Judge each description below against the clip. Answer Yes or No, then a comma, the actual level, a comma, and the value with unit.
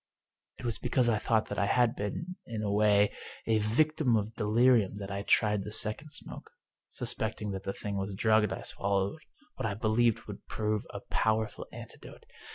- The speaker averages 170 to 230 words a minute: Yes, average, 180 wpm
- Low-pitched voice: Yes, low, 110 Hz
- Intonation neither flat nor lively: No, narrow, 2.3 semitones